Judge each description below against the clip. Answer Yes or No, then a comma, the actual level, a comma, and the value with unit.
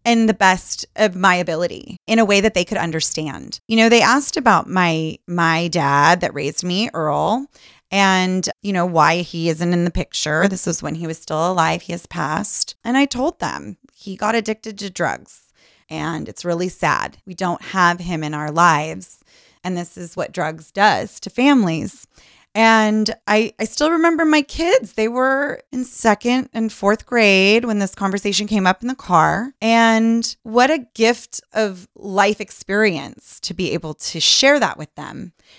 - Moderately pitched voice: No, high, 200 Hz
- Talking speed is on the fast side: No, average, 185 wpm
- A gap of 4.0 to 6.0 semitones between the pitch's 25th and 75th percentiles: Yes, average, 4.6 semitones